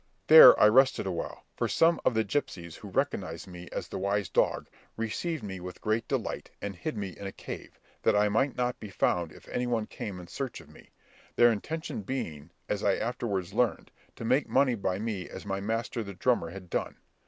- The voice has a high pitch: No, low, 105 Hz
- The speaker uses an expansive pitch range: No, average, 4.5 semitones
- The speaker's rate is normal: No, fast, 210 wpm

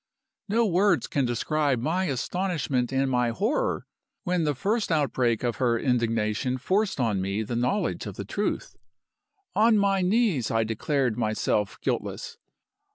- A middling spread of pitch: No, wide, 8.2 semitones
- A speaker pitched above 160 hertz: No, low, 135 Hz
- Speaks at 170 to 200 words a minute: No, average, 145 wpm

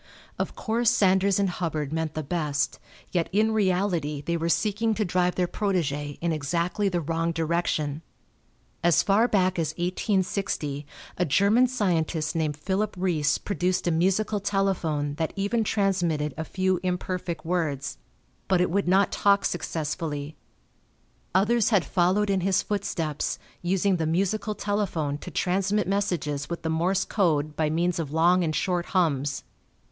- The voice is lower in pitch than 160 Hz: No, medium, 180 Hz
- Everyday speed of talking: Yes, average, 150 wpm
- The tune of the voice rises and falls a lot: No, average, 3.7 semitones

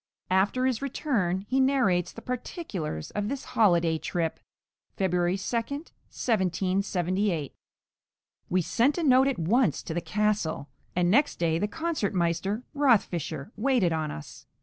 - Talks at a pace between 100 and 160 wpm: Yes, slow, 135 wpm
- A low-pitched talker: No, high, 195 Hz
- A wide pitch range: Yes, wide, 6.6 semitones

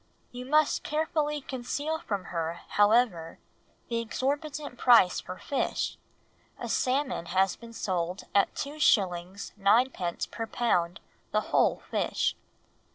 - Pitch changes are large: Yes, wide, 7.1 semitones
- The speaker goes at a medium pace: No, slow, 115 wpm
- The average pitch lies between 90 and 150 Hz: No, high, 230 Hz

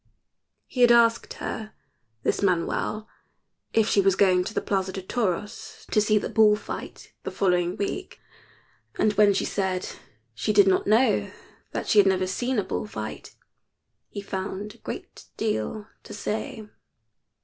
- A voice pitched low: No, high, 205 Hz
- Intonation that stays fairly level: Yes, narrow, 2.3 semitones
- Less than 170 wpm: Yes, average, 160 wpm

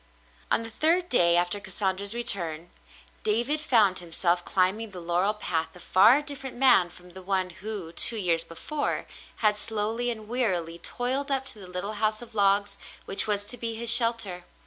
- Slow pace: No, average, 175 wpm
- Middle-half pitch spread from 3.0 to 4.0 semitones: No, average, 4.5 semitones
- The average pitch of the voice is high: Yes, high, 205 Hz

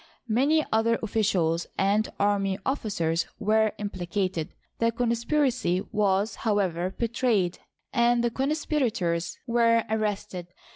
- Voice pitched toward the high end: Yes, high, 215 Hz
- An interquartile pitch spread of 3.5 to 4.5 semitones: Yes, average, 3.8 semitones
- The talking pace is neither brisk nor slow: No, slow, 105 wpm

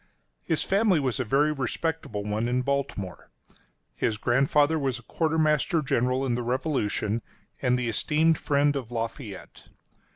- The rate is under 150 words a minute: Yes, average, 140 wpm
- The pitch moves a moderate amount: Yes, average, 4.3 semitones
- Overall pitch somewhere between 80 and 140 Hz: Yes, low, 135 Hz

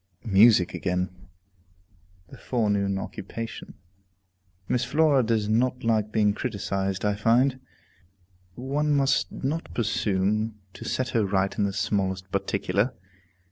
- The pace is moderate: No, slow, 115 wpm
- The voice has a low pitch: Yes, low, 110 Hz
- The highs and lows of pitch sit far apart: No, average, 4.2 semitones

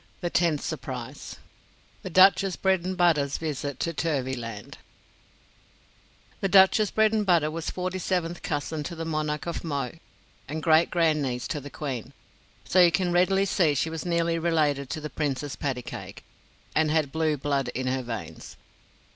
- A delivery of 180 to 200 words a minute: No, average, 145 wpm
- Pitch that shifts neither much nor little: Yes, average, 3.6 semitones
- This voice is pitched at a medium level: Yes, medium, 160 Hz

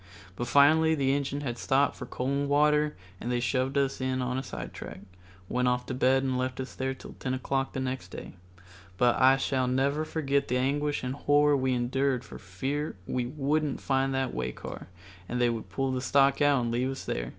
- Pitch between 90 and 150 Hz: Yes, low, 135 Hz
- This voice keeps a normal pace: No, fast, 215 wpm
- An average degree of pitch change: No, narrow, 1.9 semitones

